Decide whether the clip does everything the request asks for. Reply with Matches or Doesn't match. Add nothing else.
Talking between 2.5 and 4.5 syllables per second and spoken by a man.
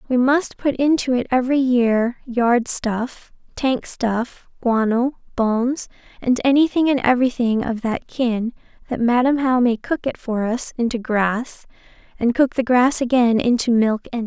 Doesn't match